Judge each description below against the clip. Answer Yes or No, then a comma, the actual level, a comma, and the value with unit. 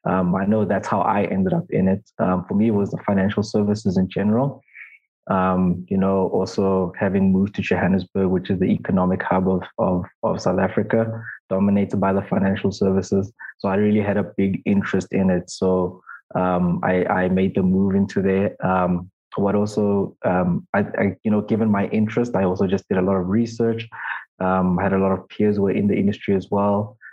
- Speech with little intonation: Yes, narrow, 1.8 semitones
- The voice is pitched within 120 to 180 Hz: No, very low, 95 Hz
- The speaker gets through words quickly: Yes, fast, 210 wpm